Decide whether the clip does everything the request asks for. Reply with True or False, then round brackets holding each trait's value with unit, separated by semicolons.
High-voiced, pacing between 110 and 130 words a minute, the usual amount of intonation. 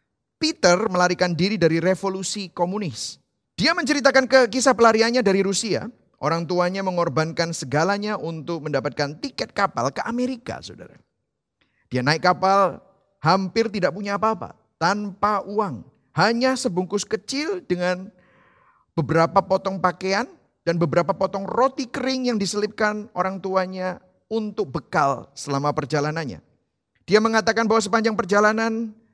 True (195 Hz; 120 wpm; 4.3 semitones)